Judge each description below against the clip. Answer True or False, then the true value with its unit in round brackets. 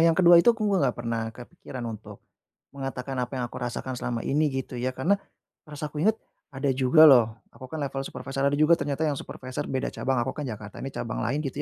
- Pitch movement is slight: False (3.3 semitones)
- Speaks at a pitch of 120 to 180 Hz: True (135 Hz)